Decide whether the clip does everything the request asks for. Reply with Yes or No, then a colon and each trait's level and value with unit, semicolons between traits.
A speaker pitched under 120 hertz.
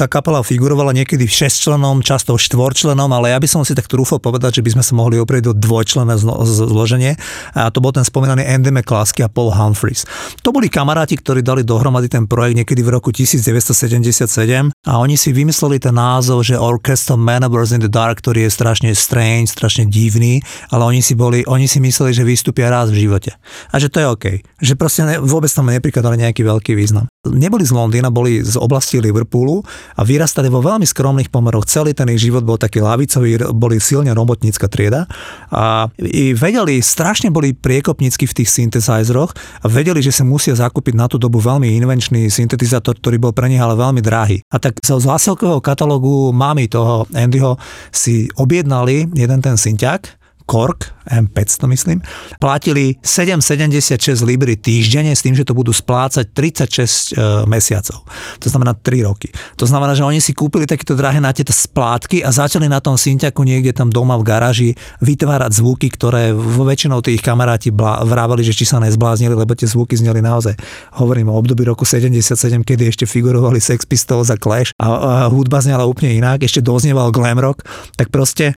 No: low, 125 Hz